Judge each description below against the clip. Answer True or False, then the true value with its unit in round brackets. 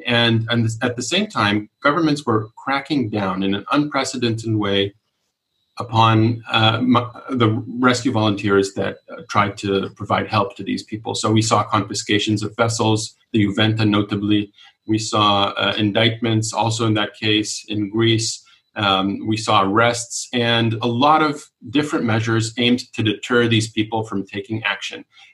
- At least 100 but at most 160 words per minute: True (150 wpm)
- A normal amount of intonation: False (2.2 semitones)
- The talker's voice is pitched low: True (110 Hz)